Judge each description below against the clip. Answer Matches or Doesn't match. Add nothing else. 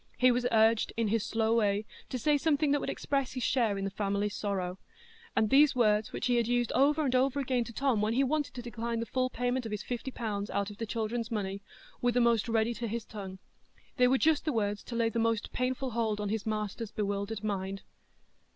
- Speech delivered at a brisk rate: Matches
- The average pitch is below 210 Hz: Doesn't match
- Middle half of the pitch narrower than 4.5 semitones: Matches